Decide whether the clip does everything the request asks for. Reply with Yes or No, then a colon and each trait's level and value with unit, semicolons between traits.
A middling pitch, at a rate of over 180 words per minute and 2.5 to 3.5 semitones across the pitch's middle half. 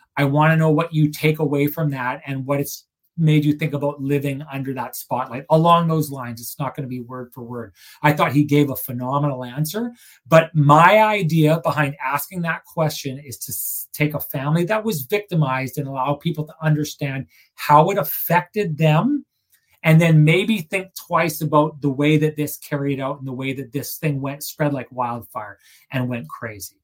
Yes: medium, 150 Hz; average, 195 wpm; average, 2.8 semitones